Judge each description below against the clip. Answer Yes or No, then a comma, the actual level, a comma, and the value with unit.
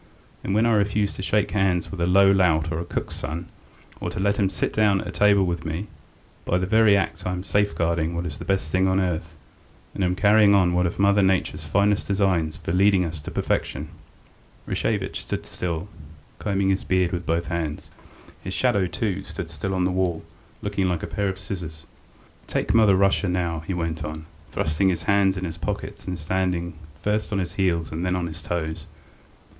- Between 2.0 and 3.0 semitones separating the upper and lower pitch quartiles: Yes, average, 2.7 semitones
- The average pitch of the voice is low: Yes, very low, 90 Hz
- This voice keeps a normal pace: No, fast, 210 wpm